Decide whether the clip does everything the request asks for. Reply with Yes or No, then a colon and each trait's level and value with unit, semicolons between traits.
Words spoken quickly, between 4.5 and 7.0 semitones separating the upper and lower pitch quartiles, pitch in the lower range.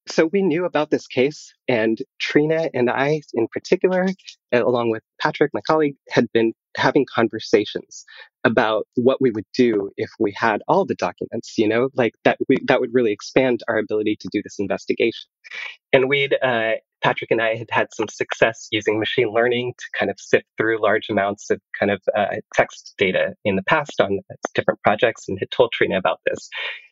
No: average, 190 wpm; average, 5.1 semitones; low, 125 Hz